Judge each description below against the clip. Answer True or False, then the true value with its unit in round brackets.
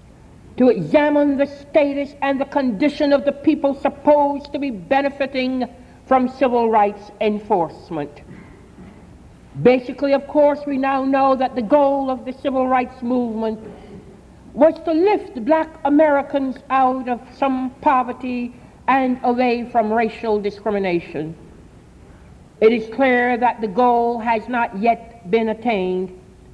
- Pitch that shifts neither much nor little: True (3.3 semitones)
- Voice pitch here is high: True (255 Hz)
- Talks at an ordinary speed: False (130 wpm)